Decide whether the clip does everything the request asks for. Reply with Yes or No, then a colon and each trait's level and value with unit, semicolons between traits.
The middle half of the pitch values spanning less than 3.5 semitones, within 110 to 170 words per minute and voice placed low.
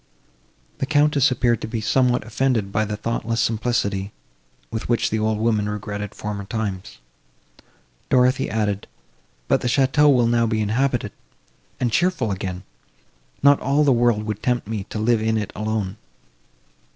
Yes: average, 2.9 semitones; average, 150 wpm; low, 110 Hz